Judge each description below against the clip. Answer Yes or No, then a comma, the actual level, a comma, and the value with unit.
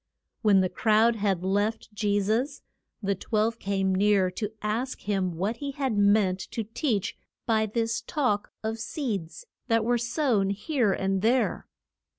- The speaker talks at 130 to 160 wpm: Yes, average, 155 wpm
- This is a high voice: Yes, high, 215 Hz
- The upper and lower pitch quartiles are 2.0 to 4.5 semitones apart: Yes, average, 2.8 semitones